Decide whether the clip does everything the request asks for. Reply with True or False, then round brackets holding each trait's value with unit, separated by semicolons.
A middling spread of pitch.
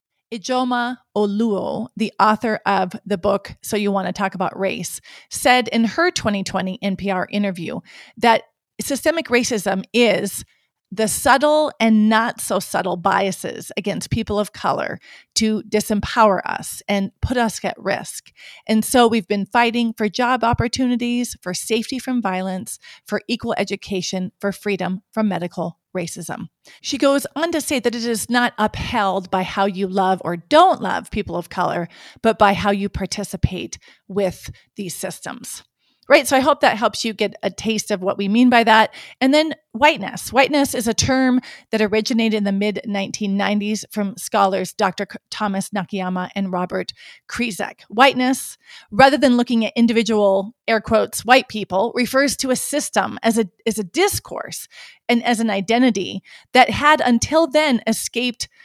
True (3.6 semitones)